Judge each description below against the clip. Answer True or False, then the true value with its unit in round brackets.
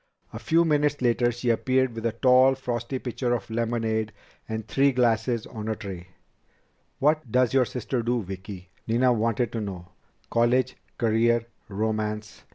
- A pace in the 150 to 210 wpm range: True (155 wpm)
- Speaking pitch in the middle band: False (115 Hz)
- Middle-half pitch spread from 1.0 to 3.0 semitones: True (2.5 semitones)